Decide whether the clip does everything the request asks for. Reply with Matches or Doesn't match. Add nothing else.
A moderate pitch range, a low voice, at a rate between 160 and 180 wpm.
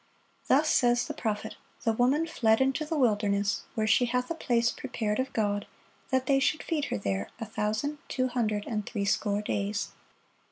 Doesn't match